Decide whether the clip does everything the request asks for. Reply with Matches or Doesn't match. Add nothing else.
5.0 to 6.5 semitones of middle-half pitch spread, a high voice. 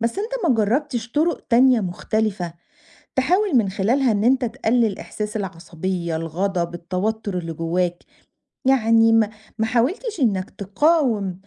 Matches